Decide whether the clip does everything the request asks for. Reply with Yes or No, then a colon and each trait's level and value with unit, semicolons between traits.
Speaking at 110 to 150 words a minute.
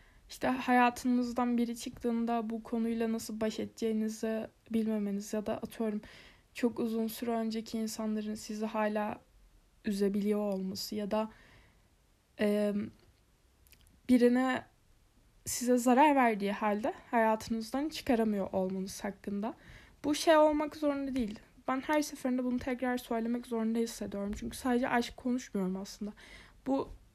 Yes: average, 115 wpm